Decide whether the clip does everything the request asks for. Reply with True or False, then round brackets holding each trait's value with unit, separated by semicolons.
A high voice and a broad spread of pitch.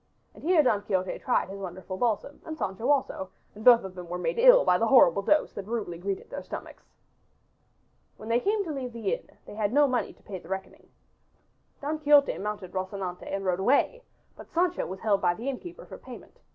True (215 Hz; 7.0 semitones)